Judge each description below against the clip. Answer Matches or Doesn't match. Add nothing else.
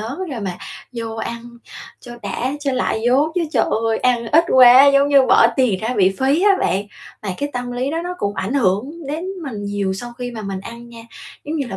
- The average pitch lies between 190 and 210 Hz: Doesn't match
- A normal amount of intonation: Matches